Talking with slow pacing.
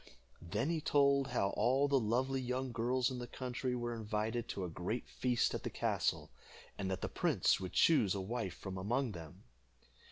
No: average, 190 wpm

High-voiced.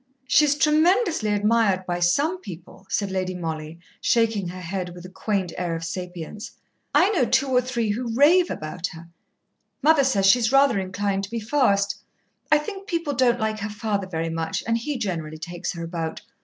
Yes: high, 205 Hz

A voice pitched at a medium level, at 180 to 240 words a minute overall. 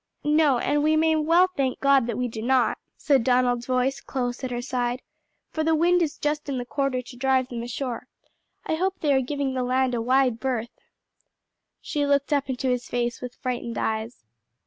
No: very high, 260 Hz; average, 200 wpm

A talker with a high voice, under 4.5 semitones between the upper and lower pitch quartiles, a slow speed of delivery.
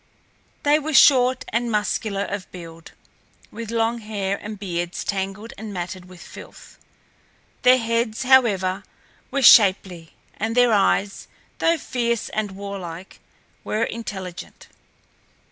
Yes: high, 210 Hz; average, 3.5 semitones; slow, 120 wpm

